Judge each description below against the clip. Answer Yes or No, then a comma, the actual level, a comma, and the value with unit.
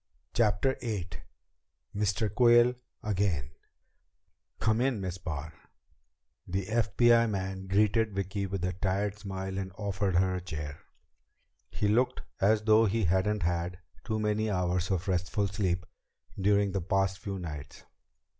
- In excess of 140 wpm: No, slow, 135 wpm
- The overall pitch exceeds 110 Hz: No, very low, 95 Hz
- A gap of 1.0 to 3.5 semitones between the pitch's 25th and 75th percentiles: Yes, narrow, 2.5 semitones